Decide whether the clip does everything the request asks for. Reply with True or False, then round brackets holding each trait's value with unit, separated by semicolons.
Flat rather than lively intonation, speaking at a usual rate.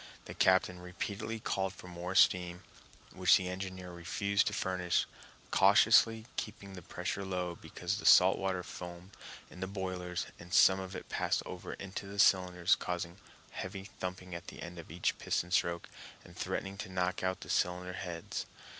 True (1.4 semitones; 170 wpm)